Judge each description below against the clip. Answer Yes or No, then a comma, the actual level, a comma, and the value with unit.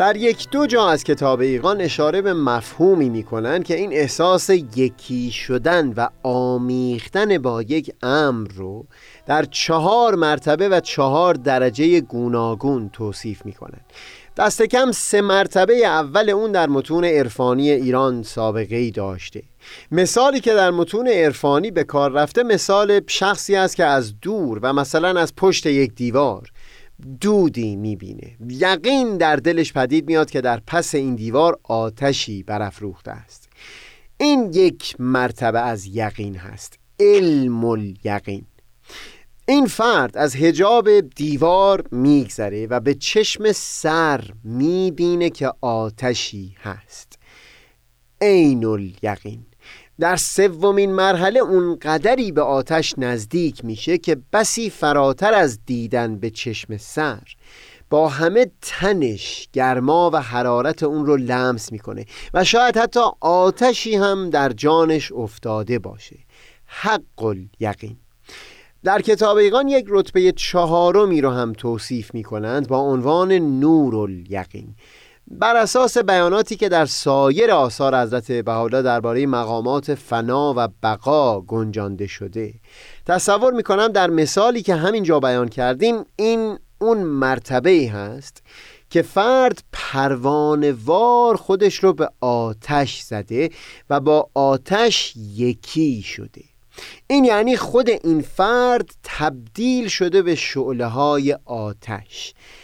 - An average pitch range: No, wide, 7.8 semitones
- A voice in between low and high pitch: Yes, medium, 145 Hz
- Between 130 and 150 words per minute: No, average, 120 wpm